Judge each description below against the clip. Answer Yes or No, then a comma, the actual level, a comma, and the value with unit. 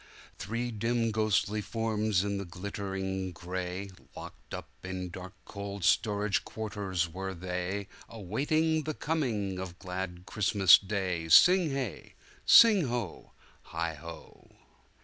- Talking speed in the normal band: No, slow, 110 wpm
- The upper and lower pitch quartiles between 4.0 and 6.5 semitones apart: No, average, 3.3 semitones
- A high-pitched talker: No, low, 100 Hz